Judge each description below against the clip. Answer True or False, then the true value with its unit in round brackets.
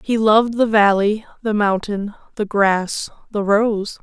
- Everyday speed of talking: True (150 wpm)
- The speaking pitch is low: False (210 Hz)